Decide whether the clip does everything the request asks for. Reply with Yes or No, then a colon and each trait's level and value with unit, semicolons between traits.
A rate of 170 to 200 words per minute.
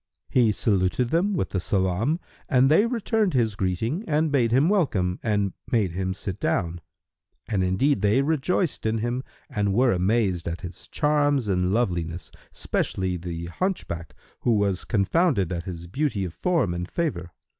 No: average, 160 wpm